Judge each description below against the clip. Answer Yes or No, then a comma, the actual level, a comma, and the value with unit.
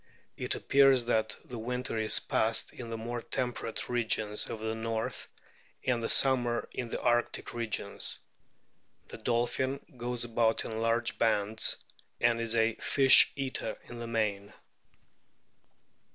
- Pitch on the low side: Yes, low, 115 Hz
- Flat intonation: Yes, narrow, 1.6 semitones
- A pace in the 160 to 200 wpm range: No, average, 140 wpm